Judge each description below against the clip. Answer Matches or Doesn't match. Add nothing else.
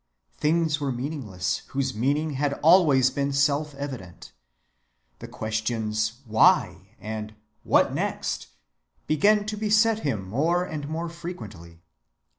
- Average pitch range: Doesn't match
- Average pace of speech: Doesn't match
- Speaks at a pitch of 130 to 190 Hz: Matches